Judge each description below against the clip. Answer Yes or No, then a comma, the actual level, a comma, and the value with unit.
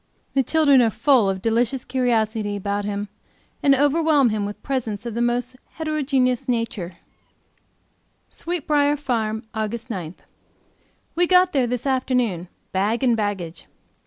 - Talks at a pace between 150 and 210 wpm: No, slow, 135 wpm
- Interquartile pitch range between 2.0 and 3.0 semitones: No, average, 4.5 semitones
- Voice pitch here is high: Yes, high, 240 Hz